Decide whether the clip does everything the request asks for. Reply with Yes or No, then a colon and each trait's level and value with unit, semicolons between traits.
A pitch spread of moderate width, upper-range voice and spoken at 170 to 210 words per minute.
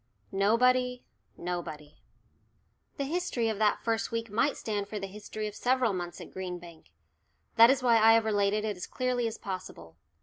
Yes: average, 3.9 semitones; high, 215 Hz; average, 175 wpm